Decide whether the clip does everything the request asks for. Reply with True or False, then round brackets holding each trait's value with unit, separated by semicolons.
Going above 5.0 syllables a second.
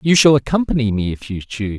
True (6.3 syllables/s)